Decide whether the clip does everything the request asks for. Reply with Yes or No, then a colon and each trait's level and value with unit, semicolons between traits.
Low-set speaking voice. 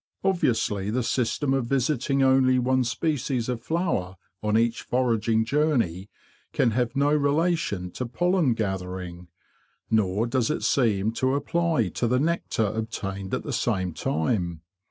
Yes: low, 120 Hz